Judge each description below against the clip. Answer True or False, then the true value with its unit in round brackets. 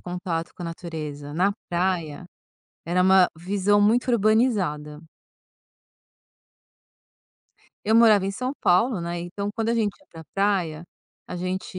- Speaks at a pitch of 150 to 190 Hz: True (185 Hz)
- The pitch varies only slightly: False (3.3 semitones)